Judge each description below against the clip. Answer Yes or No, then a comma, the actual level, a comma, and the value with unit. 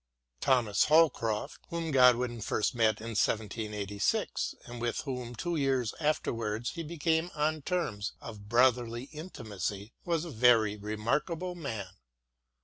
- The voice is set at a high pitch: No, low, 120 Hz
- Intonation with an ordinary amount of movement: No, wide, 5.9 semitones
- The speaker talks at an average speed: No, slow, 125 wpm